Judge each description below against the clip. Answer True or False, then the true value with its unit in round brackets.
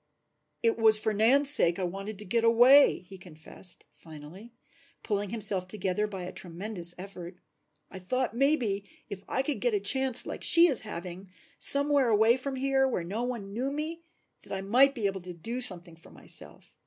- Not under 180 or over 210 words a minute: True (190 wpm)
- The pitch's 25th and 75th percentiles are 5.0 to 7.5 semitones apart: True (5.3 semitones)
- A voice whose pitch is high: True (210 Hz)